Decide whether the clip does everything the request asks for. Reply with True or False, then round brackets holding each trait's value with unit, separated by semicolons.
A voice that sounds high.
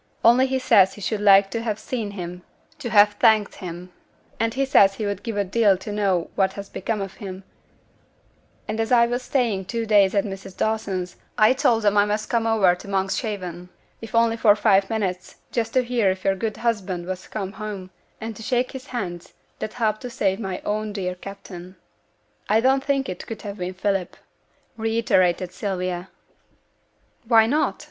True (205 Hz)